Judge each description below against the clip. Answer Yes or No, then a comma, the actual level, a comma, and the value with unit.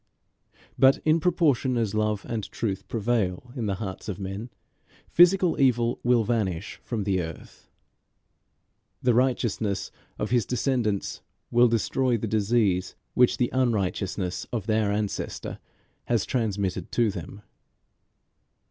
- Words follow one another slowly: Yes, slow, 125 wpm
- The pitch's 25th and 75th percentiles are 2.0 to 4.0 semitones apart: Yes, average, 3.6 semitones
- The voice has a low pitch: Yes, low, 110 Hz